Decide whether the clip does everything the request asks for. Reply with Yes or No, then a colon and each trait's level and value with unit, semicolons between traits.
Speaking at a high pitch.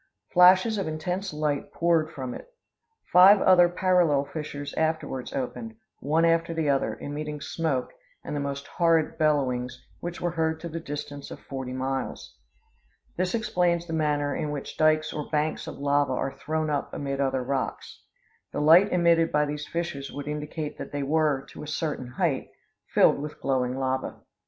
No: medium, 150 Hz